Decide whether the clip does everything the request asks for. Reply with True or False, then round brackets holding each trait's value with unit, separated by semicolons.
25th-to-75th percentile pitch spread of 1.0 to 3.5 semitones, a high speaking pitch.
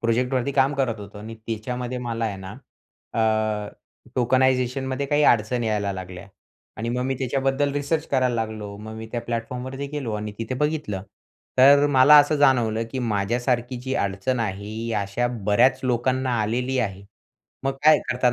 False (3.2 semitones; 120 Hz)